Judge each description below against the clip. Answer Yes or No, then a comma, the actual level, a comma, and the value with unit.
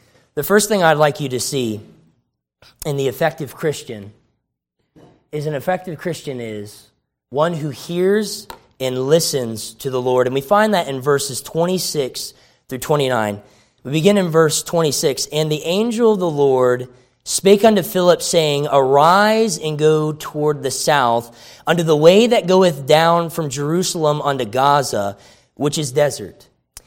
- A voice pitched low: No, medium, 150 Hz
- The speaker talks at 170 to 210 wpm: No, average, 150 wpm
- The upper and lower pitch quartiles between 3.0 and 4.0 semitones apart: No, average, 4.8 semitones